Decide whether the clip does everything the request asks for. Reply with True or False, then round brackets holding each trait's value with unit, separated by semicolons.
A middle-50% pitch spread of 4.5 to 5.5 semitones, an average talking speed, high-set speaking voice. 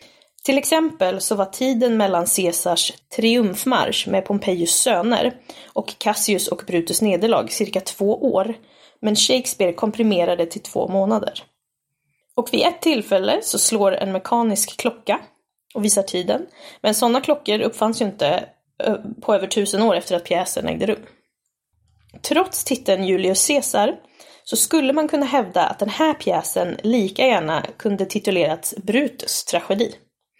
True (5.2 semitones; 140 wpm; 215 Hz)